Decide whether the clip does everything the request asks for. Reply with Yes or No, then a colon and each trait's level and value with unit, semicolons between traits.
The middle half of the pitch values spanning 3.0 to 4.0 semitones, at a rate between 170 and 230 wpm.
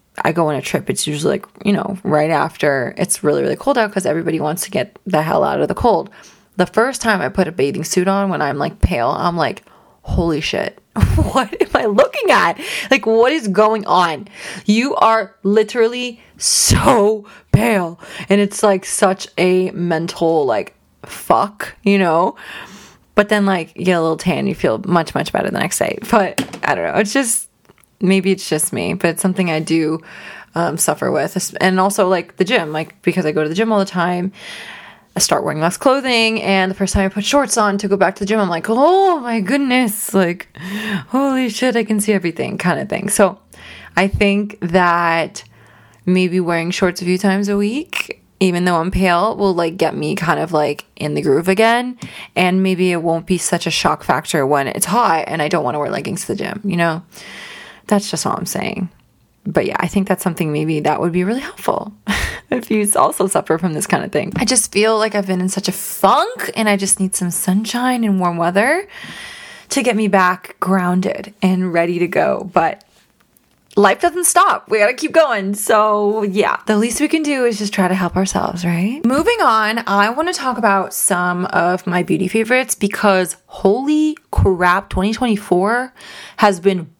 Yes: average, 3.5 semitones; fast, 205 wpm